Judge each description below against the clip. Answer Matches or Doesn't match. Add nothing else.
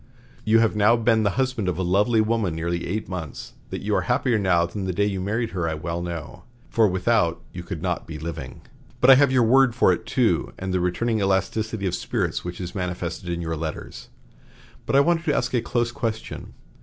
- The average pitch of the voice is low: Matches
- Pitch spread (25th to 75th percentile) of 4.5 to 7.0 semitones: Matches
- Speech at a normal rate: Doesn't match